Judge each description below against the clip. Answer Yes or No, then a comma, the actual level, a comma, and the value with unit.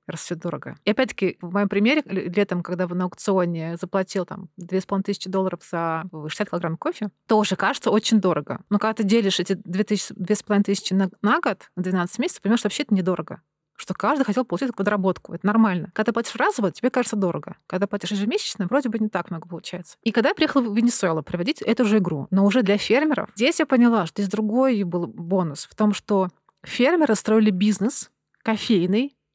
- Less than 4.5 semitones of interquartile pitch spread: Yes, average, 3.3 semitones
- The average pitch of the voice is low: No, high, 200 Hz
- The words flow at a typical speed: No, fast, 190 wpm